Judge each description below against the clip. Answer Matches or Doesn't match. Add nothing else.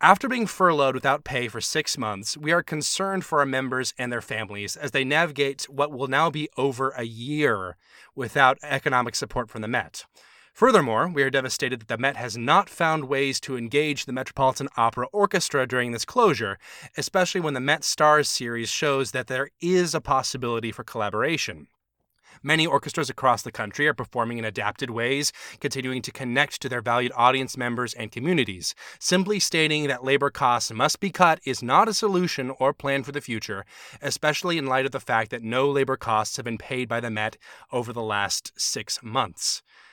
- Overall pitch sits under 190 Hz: Matches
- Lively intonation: Doesn't match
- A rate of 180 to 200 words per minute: Matches